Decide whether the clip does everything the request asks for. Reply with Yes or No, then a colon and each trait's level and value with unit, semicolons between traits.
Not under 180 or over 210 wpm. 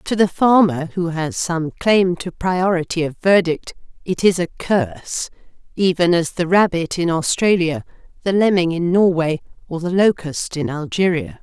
No: average, 160 wpm